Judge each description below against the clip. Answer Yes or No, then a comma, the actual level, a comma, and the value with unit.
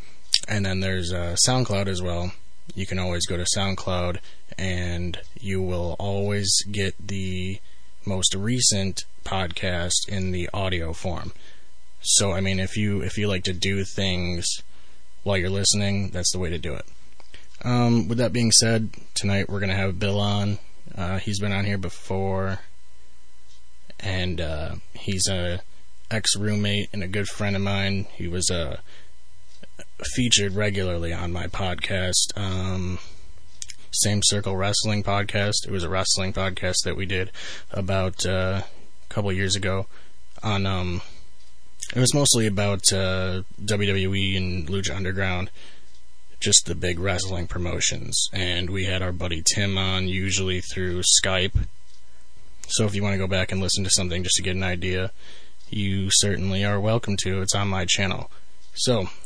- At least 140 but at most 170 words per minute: Yes, average, 155 wpm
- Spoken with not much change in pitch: Yes, narrow, 1.8 semitones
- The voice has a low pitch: Yes, very low, 95 Hz